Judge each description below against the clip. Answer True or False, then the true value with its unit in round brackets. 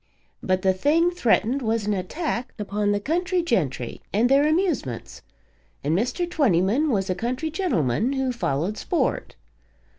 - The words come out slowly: False (145 wpm)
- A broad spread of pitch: True (8.2 semitones)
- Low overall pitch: False (235 Hz)